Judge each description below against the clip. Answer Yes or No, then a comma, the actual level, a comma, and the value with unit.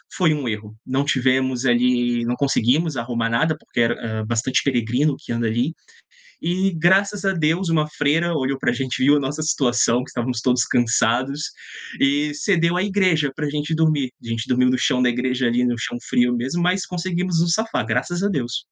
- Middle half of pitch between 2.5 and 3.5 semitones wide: No, average, 5.1 semitones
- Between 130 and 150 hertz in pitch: Yes, low, 135 Hz